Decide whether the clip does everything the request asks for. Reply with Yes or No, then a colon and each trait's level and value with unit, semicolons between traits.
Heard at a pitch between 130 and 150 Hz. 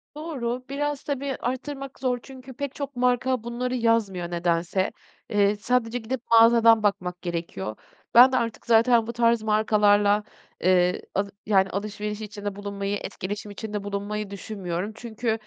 No: high, 220 Hz